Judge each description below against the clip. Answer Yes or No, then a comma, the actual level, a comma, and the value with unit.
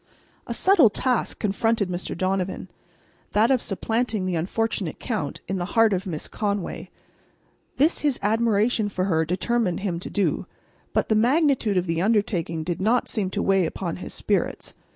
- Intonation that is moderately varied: Yes, average, 3.9 semitones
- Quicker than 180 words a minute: No, average, 160 wpm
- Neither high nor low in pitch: No, high, 200 Hz